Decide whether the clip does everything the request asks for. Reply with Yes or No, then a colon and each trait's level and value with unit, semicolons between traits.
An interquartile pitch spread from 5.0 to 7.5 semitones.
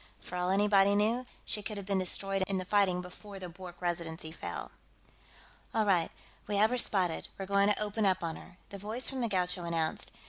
No: narrow, 2.5 semitones